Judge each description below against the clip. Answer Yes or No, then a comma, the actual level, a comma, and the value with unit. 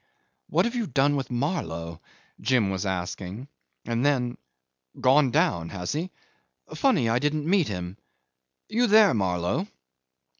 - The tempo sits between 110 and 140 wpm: Yes, slow, 135 wpm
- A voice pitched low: Yes, low, 125 Hz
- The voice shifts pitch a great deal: Yes, wide, 8.4 semitones